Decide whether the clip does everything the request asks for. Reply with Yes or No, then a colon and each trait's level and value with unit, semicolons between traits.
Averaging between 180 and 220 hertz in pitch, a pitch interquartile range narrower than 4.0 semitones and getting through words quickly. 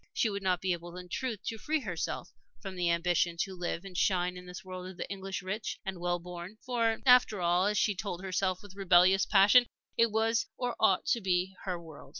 Yes: high, 190 Hz; average, 2.9 semitones; fast, 220 wpm